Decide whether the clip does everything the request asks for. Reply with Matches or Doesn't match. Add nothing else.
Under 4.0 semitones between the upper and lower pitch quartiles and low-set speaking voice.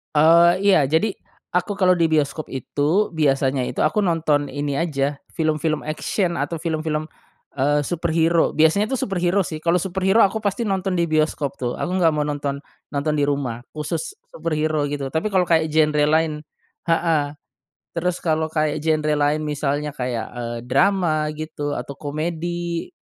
Doesn't match